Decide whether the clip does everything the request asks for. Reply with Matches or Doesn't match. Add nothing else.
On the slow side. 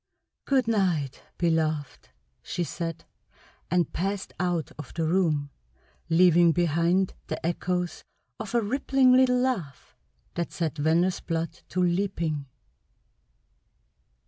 Matches